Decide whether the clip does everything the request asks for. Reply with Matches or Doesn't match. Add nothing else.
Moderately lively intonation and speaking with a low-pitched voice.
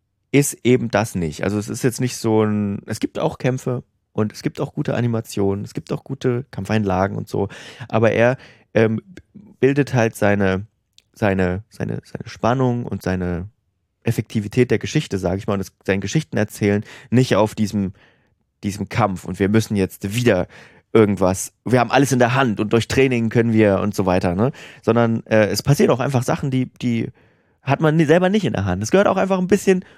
Matches